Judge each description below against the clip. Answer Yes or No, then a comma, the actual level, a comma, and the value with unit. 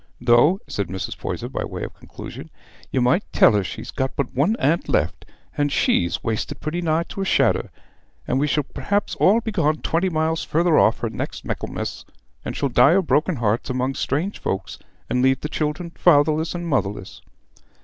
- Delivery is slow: No, average, 190 wpm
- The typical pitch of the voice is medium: Yes, medium, 150 Hz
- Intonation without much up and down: No, average, 5.1 semitones